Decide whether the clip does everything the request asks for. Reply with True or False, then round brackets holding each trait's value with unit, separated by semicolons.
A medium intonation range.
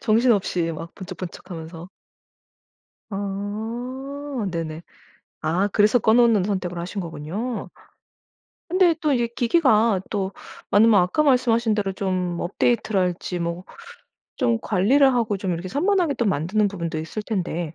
True (5.0 semitones)